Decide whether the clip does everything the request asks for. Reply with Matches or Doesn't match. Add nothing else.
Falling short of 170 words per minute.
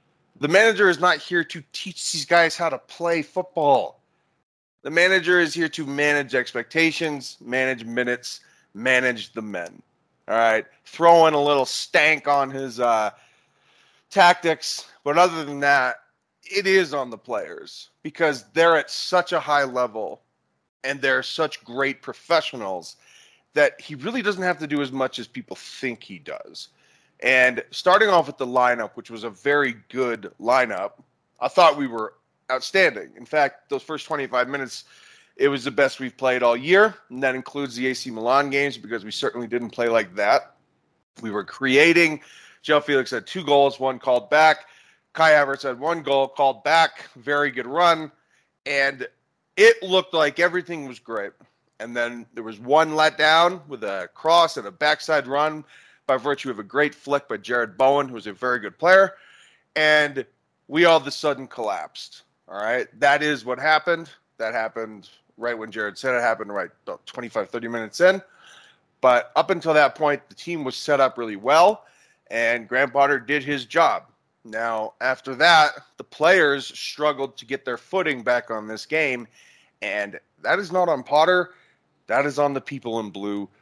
Doesn't match